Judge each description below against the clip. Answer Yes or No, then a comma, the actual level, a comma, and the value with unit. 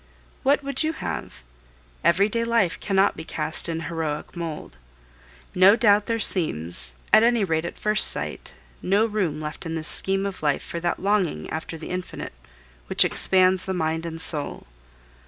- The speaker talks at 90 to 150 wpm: No, average, 165 wpm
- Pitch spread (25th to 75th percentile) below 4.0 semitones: No, average, 4.3 semitones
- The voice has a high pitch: No, medium, 180 Hz